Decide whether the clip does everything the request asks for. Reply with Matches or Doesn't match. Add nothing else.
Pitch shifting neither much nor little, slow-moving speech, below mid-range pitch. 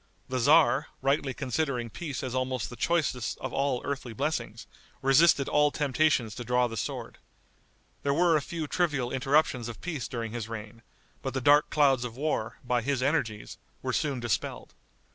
Doesn't match